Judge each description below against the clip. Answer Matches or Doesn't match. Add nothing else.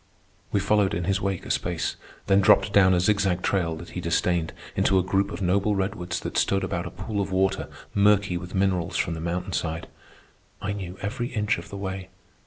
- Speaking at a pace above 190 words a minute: Matches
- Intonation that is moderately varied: Doesn't match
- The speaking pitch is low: Matches